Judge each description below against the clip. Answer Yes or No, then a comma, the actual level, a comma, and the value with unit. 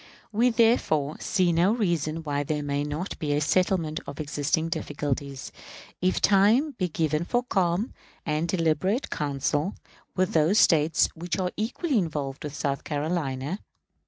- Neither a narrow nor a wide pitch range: Yes, average, 4.3 semitones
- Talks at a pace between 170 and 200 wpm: No, average, 145 wpm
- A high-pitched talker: No, medium, 165 Hz